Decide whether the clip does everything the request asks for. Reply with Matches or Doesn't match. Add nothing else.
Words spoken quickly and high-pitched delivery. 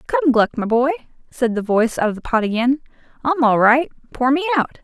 Matches